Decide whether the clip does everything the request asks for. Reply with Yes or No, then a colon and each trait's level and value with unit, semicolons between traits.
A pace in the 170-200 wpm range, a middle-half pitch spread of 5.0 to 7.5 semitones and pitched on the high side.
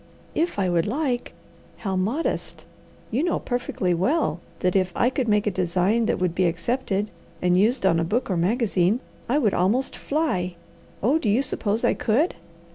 Yes: average, 180 wpm; wide, 5.5 semitones; high, 210 Hz